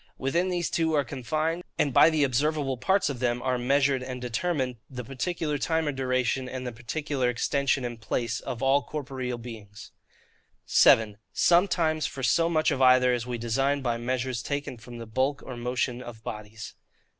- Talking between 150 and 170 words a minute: No, average, 180 wpm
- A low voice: Yes, low, 130 Hz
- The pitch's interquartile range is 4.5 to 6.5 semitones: No, average, 3.3 semitones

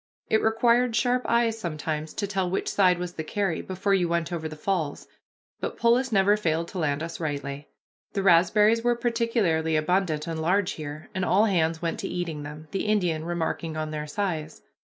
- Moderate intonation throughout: Yes, average, 4.6 semitones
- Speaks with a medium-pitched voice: Yes, medium, 175 Hz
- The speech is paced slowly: No, average, 190 wpm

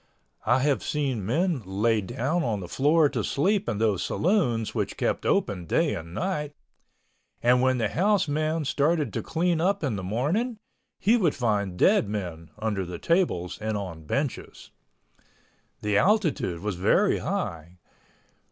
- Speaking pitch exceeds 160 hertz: No, low, 130 Hz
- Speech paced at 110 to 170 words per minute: Yes, average, 155 wpm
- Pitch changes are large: Yes, wide, 8.5 semitones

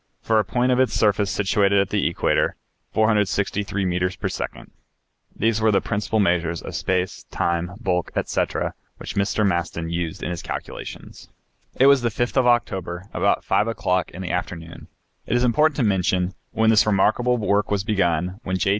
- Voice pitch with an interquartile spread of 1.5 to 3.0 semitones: No, average, 3.5 semitones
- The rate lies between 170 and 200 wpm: Yes, average, 180 wpm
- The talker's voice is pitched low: Yes, low, 100 Hz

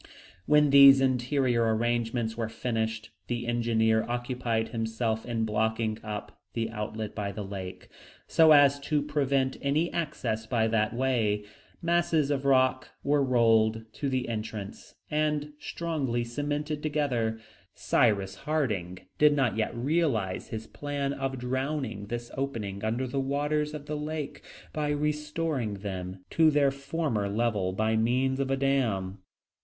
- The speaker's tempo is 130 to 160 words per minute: Yes, average, 140 wpm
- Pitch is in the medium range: No, low, 125 Hz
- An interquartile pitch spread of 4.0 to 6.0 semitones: Yes, average, 4.4 semitones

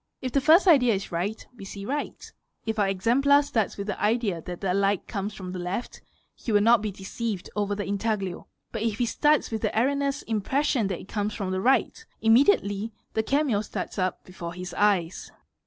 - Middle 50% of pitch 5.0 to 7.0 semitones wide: No, average, 3.7 semitones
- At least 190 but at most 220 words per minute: Yes, fast, 205 wpm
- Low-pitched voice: No, high, 210 Hz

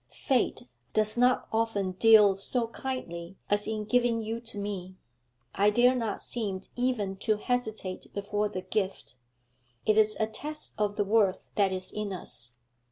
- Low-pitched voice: No, high, 210 Hz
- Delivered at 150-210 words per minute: Yes, average, 160 wpm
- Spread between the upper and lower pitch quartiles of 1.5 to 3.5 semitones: Yes, average, 2.7 semitones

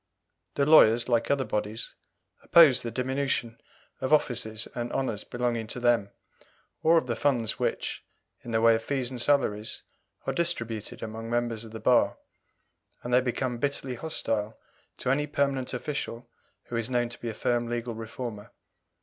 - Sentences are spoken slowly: No, average, 165 wpm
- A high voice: No, low, 120 Hz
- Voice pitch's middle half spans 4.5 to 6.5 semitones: No, average, 2.7 semitones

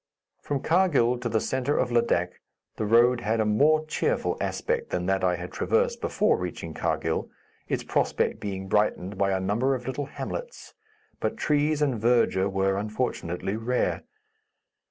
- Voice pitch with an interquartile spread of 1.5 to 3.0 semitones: No, average, 5.3 semitones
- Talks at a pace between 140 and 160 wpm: Yes, average, 155 wpm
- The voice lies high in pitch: No, low, 115 Hz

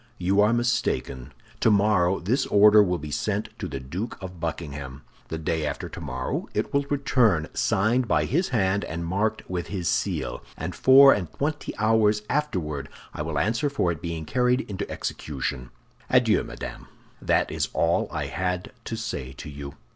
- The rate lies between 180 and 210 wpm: No, average, 170 wpm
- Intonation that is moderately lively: No, wide, 6.3 semitones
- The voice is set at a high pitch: No, very low, 95 Hz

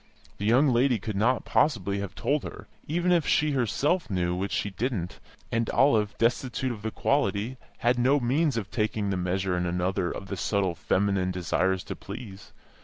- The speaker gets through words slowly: No, average, 180 wpm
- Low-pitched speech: Yes, low, 105 Hz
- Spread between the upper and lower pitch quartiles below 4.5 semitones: No, average, 5.3 semitones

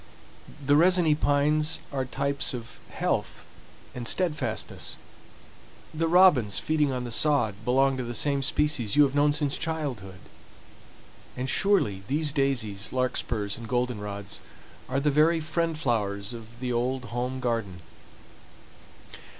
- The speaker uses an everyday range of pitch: Yes, average, 4.2 semitones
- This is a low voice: Yes, low, 130 Hz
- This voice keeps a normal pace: No, slow, 130 wpm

